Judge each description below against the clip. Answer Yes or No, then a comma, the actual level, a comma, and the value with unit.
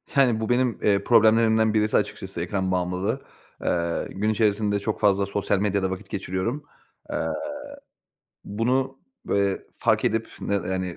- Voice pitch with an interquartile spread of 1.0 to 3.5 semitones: Yes, average, 2.7 semitones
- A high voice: No, low, 100 Hz